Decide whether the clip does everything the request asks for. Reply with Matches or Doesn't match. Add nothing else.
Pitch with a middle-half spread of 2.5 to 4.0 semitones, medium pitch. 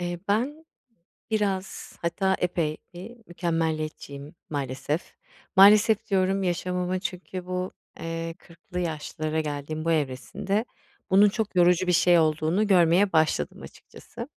Matches